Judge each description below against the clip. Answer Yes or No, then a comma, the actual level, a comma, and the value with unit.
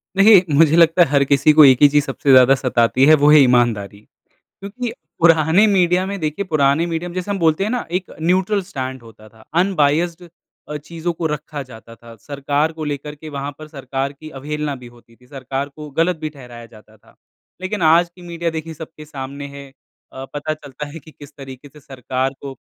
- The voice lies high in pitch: No, medium, 150 Hz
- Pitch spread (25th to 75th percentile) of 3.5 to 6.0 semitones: Yes, average, 3.8 semitones